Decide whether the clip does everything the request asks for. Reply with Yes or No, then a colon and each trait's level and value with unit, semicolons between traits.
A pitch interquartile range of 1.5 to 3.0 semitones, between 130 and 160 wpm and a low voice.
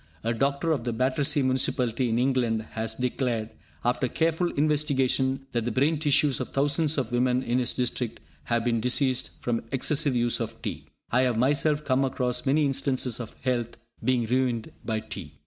No: average, 2.7 semitones; average, 175 wpm; low, 130 Hz